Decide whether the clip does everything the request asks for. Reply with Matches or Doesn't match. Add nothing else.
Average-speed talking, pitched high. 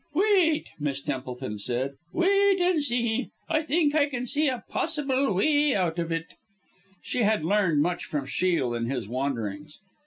Matches